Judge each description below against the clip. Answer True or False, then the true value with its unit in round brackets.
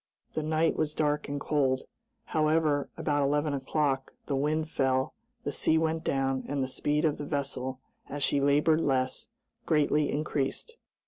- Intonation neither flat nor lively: False (2.2 semitones)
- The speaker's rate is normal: True (155 wpm)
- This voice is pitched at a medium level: True (145 Hz)